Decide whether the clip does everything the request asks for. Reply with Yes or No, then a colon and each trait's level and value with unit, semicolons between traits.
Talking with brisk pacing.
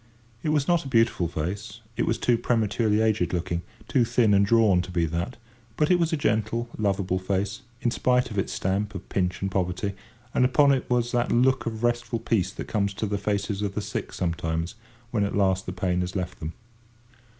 Yes: fast, 210 wpm